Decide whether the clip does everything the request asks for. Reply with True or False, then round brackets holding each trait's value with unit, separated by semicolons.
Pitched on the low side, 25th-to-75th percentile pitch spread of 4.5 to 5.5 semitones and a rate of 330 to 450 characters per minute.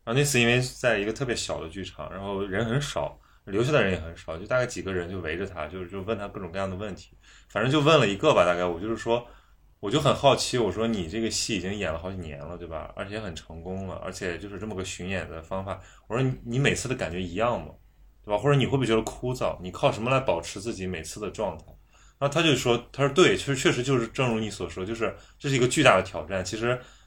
True (105 Hz; 5.1 semitones; 385 characters per minute)